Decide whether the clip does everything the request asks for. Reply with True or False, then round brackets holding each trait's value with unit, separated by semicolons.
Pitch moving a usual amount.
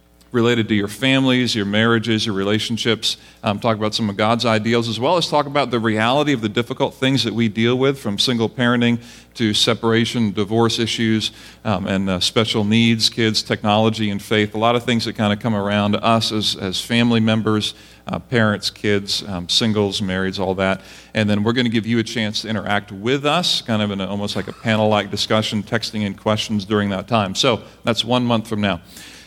False (2.1 semitones)